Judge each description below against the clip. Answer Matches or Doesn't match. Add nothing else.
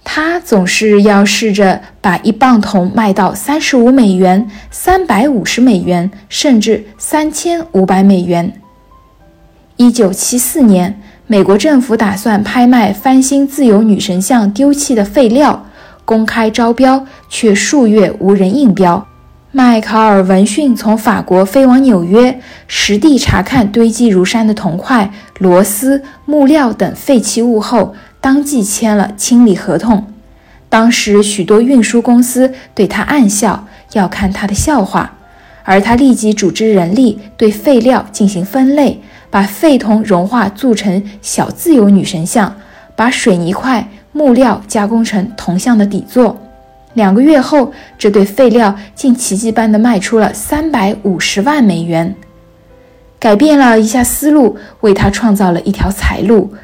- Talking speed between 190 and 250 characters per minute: Matches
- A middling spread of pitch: Matches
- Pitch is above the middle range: Matches